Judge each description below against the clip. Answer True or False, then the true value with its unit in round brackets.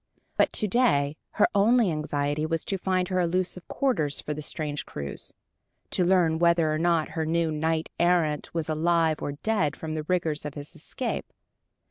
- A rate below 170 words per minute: False (175 wpm)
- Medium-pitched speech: True (165 Hz)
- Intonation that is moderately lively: True (3.0 semitones)